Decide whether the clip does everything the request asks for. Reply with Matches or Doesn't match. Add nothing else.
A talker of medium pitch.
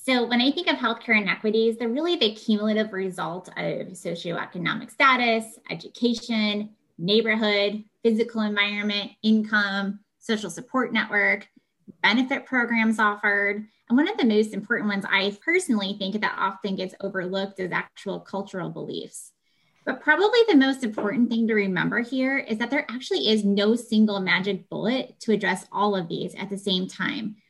Doesn't match